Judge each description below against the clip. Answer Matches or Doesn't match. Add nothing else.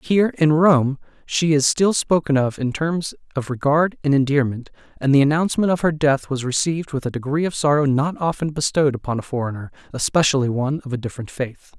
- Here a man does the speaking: Matches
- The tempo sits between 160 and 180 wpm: Doesn't match